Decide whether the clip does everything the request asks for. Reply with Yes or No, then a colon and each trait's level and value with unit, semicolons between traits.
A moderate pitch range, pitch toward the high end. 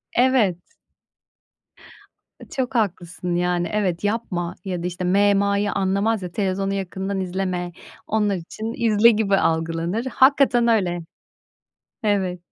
Yes: average, 3.3 semitones; high, 195 Hz